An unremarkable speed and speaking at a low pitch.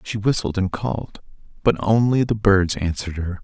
Yes: average, 175 wpm; low, 100 Hz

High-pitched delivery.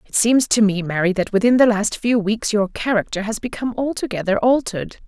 Yes: high, 215 Hz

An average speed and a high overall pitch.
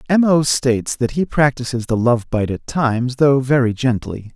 No: average, 195 wpm; low, 125 Hz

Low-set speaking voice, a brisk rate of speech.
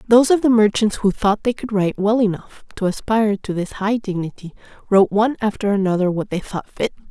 No: high, 205 Hz; fast, 210 wpm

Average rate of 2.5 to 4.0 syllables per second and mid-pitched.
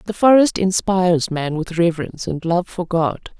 No: 5.0 syllables/s; medium, 175 Hz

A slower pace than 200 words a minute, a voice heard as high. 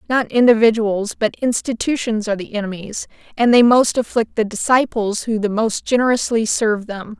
Yes: average, 160 wpm; high, 225 Hz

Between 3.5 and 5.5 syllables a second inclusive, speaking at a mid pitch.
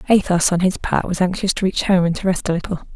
No: 6.3 syllables/s; medium, 180 Hz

